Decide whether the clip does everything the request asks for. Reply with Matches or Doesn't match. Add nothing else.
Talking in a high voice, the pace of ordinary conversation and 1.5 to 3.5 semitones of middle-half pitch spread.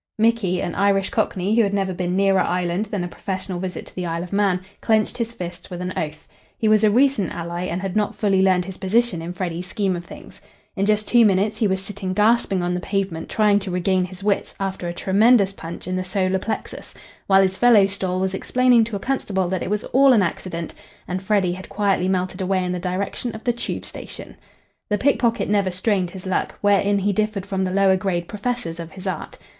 Doesn't match